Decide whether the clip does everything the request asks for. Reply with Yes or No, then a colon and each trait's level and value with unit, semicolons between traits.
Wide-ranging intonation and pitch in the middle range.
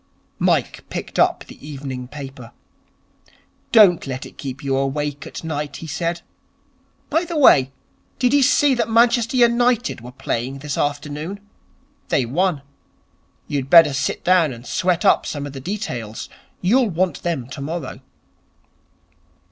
Yes: wide, 6.8 semitones; medium, 150 Hz